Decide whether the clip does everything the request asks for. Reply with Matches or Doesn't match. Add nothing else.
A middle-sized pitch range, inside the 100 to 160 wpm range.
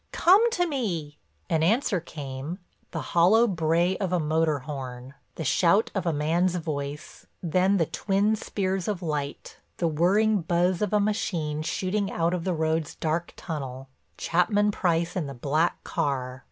Matches